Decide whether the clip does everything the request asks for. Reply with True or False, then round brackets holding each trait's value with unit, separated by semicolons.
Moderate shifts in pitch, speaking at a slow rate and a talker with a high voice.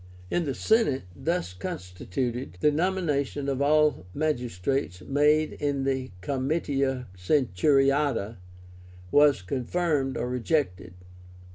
False (3.5 semitones; 100 wpm; 135 Hz)